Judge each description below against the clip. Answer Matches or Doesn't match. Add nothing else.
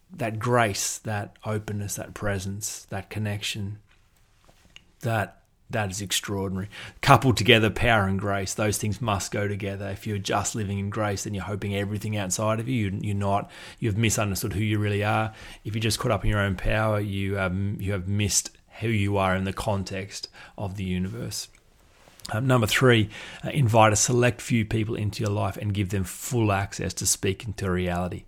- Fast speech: Doesn't match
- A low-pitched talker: Matches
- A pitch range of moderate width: Doesn't match